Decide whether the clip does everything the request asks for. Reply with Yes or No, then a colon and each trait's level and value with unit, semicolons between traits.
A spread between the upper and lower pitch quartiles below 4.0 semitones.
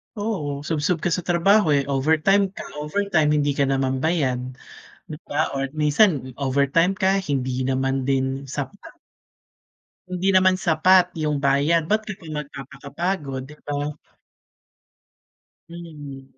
No: average, 4.3 semitones